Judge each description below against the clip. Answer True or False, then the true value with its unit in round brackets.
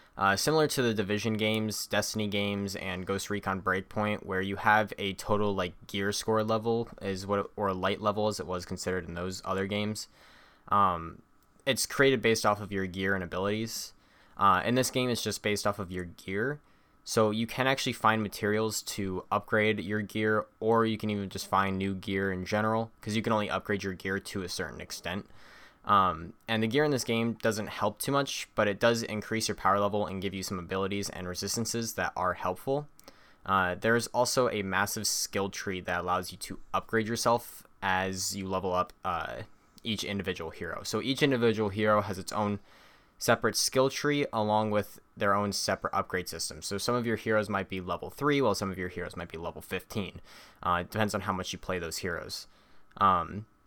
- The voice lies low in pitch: True (105 Hz)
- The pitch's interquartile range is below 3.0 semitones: True (2.6 semitones)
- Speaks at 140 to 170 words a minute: False (205 wpm)